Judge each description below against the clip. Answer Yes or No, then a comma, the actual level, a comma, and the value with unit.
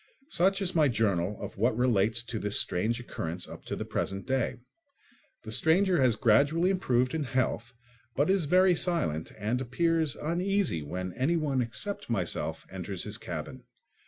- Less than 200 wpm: Yes, average, 160 wpm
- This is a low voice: Yes, low, 130 Hz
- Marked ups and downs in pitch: Yes, wide, 7.5 semitones